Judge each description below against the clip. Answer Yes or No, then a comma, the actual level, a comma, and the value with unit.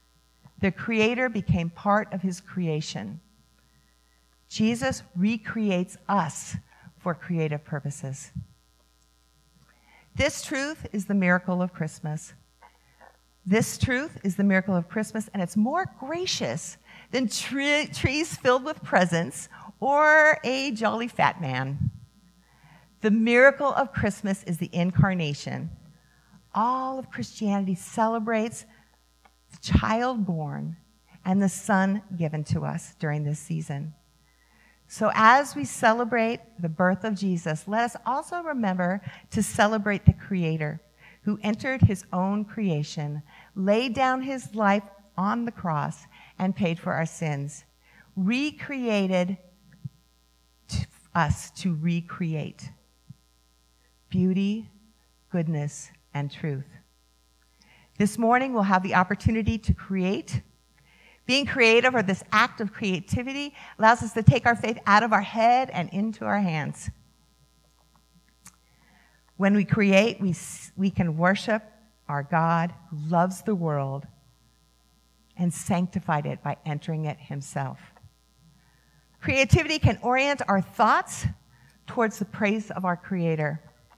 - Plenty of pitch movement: Yes, wide, 6.2 semitones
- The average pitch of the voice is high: No, medium, 180 Hz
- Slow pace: Yes, slow, 120 wpm